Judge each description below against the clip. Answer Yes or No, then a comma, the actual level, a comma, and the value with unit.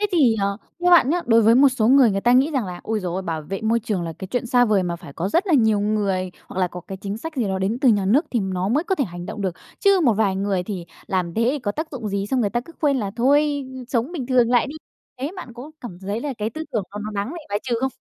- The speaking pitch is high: Yes, high, 225 Hz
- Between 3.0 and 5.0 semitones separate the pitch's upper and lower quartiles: No, wide, 5.4 semitones